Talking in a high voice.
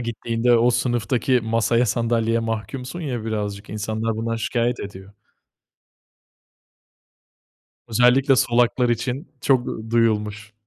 No: low, 115 Hz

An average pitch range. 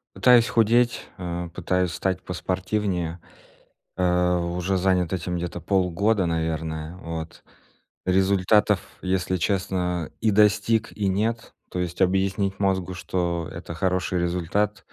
No: narrow, 2.1 semitones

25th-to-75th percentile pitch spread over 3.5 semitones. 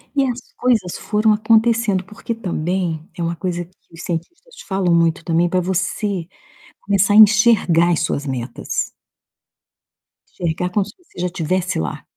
Yes: average, 4.0 semitones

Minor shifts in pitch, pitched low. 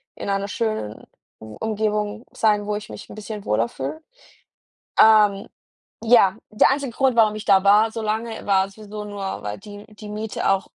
No: narrow, 1.8 semitones; high, 210 Hz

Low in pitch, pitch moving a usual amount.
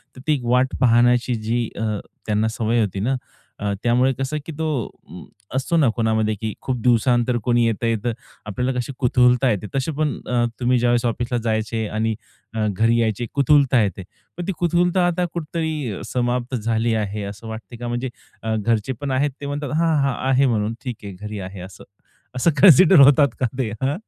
Yes: low, 120 Hz; average, 3.3 semitones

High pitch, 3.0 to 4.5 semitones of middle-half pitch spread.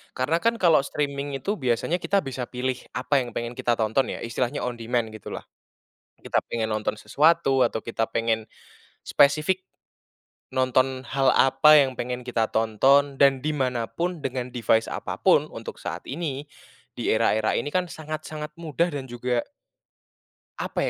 No: low, 130 Hz; average, 4.0 semitones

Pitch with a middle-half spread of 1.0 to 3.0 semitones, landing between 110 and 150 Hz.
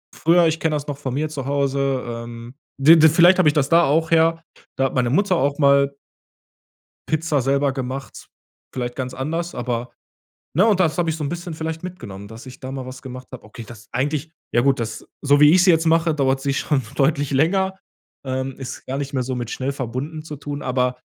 No: average, 3.8 semitones; medium, 140 Hz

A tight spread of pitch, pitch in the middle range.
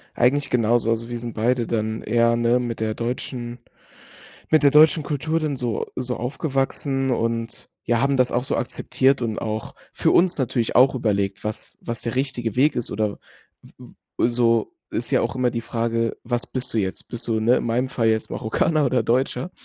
No: narrow, 2.3 semitones; low, 120 Hz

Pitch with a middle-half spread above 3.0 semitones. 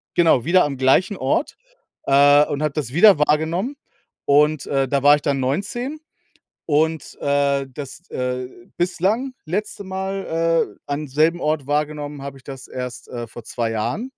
Yes: average, 4.0 semitones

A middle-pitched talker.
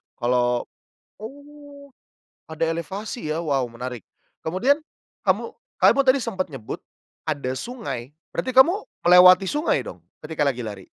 Yes: medium, 165 Hz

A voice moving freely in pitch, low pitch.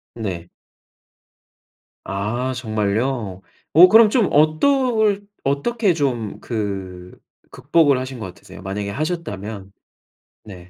Yes: wide, 8.5 semitones; low, 120 Hz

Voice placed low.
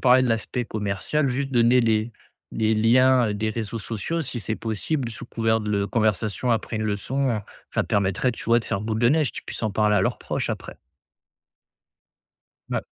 Yes: low, 115 Hz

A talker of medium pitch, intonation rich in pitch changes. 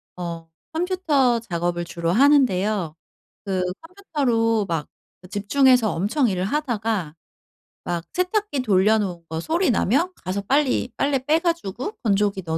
No: high, 220 Hz; wide, 7.7 semitones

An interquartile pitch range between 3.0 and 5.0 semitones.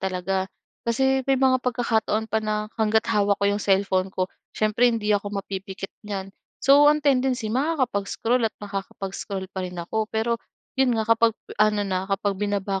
Yes: average, 3.4 semitones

